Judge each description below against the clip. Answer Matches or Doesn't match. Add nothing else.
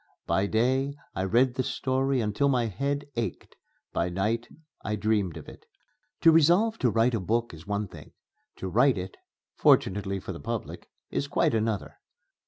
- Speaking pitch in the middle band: Doesn't match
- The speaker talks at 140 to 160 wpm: Doesn't match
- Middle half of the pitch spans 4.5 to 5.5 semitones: Matches